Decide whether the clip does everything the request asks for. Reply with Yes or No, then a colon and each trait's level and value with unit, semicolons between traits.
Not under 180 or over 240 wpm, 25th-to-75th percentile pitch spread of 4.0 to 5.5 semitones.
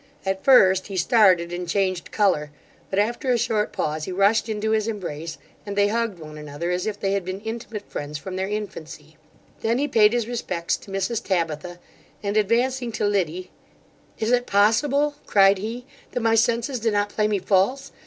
No: average, 190 wpm; average, 3.6 semitones